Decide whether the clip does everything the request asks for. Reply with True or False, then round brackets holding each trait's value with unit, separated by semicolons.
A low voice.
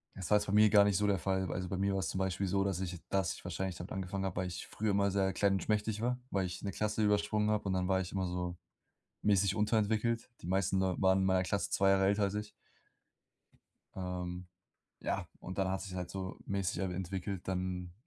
True (95 Hz)